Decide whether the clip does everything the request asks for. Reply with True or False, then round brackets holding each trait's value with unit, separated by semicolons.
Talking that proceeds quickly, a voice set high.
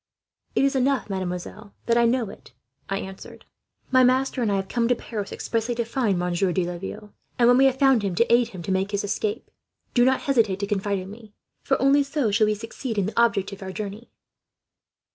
True (220 wpm; 220 Hz)